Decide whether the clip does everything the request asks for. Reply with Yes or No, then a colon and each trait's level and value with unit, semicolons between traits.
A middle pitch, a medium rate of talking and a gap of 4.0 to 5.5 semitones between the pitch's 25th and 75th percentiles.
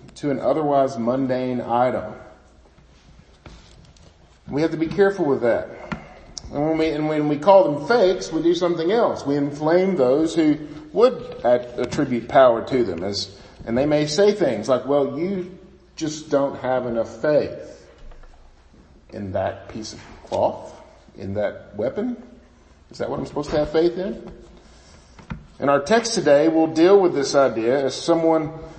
Yes: medium, 150 Hz; average, 160 wpm; average, 4.9 semitones